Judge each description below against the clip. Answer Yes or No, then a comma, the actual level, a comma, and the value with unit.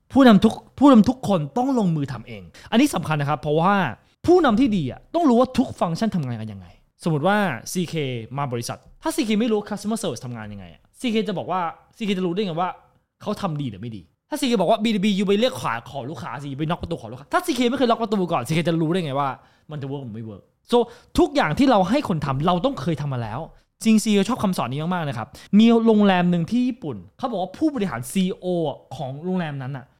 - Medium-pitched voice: Yes, medium, 180 Hz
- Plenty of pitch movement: Yes, wide, 8.4 semitones